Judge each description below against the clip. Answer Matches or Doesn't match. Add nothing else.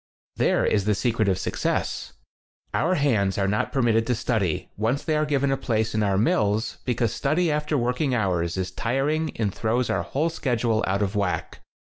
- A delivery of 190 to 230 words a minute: Matches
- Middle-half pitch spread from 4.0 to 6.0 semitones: Matches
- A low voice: Matches